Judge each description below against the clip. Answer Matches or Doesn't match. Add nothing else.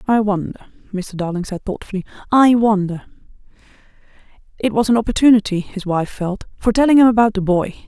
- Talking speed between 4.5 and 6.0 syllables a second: Matches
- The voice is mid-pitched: Doesn't match